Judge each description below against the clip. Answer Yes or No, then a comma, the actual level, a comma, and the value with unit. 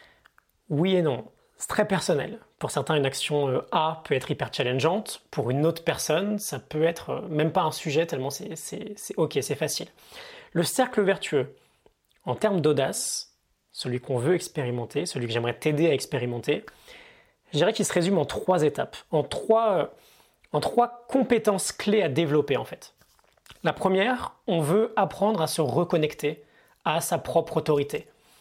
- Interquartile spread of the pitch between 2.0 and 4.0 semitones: No, wide, 5.5 semitones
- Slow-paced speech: No, average, 165 wpm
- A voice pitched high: No, medium, 160 Hz